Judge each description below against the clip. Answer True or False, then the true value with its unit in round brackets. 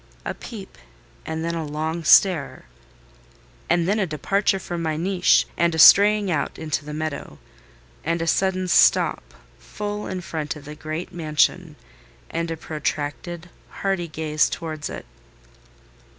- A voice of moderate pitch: True (165 Hz)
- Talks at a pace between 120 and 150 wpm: True (145 wpm)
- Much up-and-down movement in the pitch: False (3.1 semitones)